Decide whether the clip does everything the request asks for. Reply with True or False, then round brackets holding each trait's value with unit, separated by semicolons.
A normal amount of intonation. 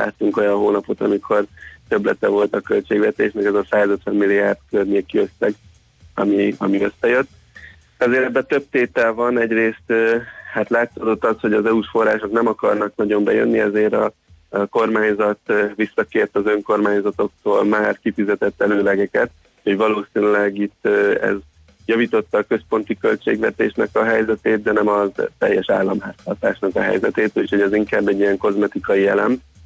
False (1.7 semitones)